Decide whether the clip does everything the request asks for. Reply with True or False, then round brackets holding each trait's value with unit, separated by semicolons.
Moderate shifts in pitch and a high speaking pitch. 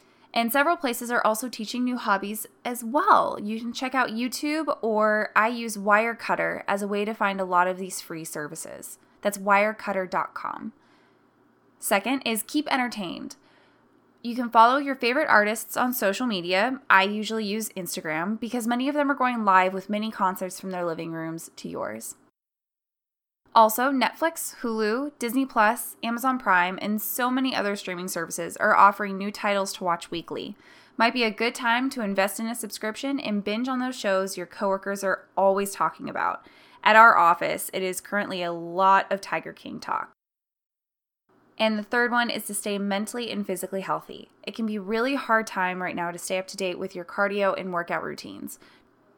True (3.9 semitones; 215 Hz)